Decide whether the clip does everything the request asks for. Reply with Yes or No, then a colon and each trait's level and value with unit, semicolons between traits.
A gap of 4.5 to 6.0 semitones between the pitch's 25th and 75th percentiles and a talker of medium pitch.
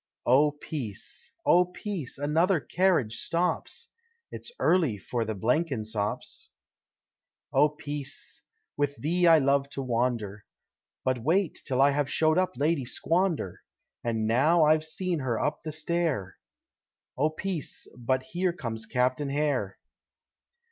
Yes: average, 5.0 semitones; medium, 145 Hz